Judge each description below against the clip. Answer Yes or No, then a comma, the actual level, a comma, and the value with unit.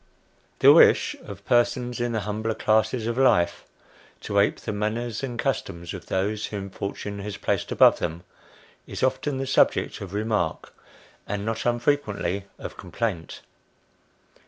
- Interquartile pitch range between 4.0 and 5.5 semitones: No, average, 3.2 semitones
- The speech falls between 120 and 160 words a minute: Yes, average, 145 wpm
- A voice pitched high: No, low, 110 Hz